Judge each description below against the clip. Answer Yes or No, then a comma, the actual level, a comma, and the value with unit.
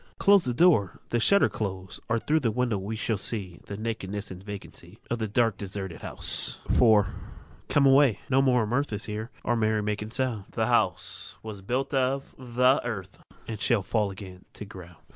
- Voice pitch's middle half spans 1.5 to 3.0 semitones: No, average, 3.8 semitones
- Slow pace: No, average, 190 wpm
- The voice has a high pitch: No, low, 110 Hz